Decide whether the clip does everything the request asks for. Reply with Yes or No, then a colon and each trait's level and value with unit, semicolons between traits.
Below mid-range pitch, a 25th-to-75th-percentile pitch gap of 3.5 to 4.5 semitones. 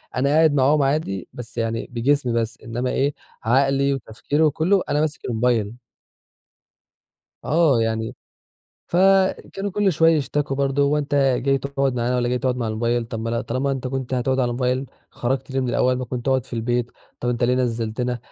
No: low, 130 Hz; average, 2.8 semitones